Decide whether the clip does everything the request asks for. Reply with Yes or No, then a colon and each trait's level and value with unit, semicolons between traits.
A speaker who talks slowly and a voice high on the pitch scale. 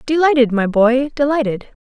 Yes: slow, 130 wpm; very high, 255 Hz